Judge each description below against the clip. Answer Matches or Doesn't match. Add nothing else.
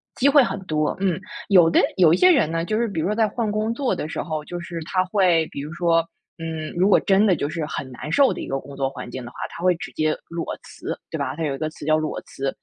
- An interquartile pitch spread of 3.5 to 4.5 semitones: Matches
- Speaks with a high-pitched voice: Doesn't match